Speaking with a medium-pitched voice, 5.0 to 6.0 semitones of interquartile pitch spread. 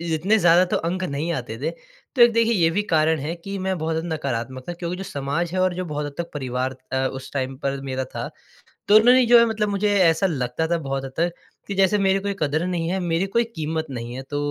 Yes: medium, 165 Hz; wide, 5.5 semitones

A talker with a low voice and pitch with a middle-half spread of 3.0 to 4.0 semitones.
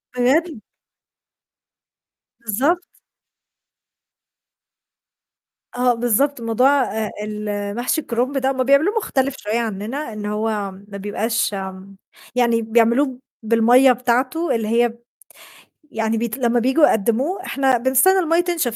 No: high, 240 Hz; average, 3.6 semitones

